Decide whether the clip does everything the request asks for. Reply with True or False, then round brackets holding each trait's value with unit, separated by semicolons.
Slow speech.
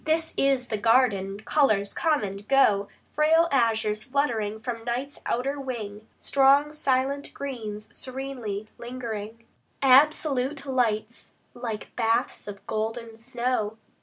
True (115 wpm)